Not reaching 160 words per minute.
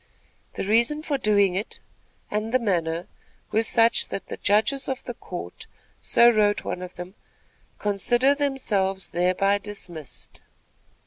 Yes: slow, 135 wpm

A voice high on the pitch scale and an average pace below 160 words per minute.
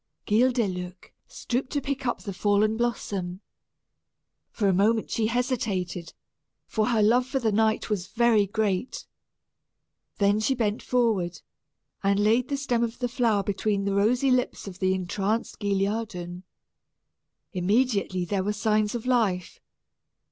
Yes: high, 215 Hz; average, 140 wpm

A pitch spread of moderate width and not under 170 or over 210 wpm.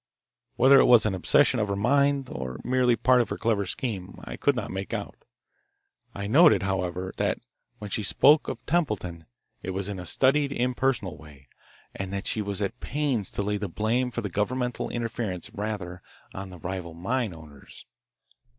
Yes: average, 5.0 semitones; average, 180 wpm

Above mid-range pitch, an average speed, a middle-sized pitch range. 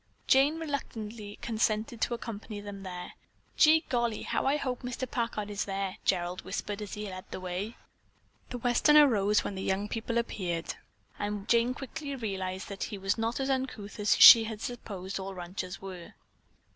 Yes: high, 210 Hz; average, 170 wpm; average, 3.8 semitones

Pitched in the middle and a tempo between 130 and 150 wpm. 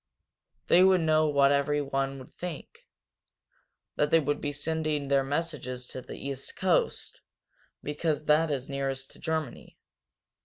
Yes: medium, 145 Hz; average, 140 wpm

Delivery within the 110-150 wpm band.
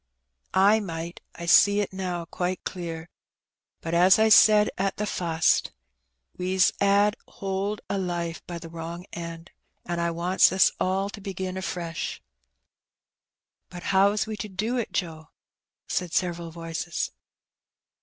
Yes: average, 145 wpm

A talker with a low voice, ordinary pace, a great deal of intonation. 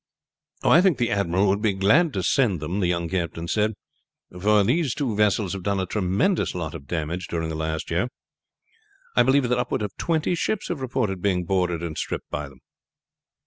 Yes: very low, 95 Hz; average, 195 wpm; wide, 5.8 semitones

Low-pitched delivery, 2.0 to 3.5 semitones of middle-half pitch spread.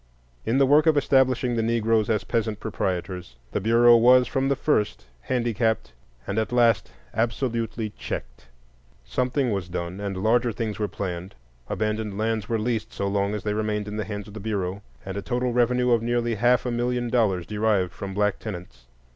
Yes: low, 110 Hz; average, 3.1 semitones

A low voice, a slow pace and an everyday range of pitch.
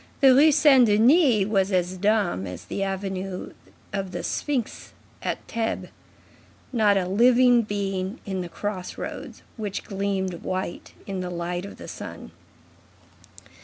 No: high, 195 Hz; slow, 130 wpm; average, 3.3 semitones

